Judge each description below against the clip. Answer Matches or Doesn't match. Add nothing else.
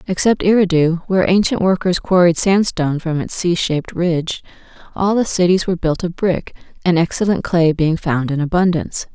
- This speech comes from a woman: Matches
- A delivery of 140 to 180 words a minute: Matches